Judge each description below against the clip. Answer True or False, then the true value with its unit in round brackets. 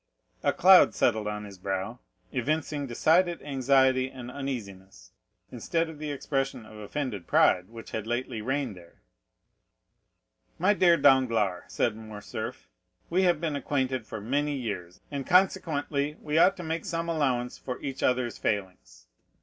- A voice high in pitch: False (130 Hz)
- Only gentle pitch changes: False (5.4 semitones)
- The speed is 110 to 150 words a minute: True (145 wpm)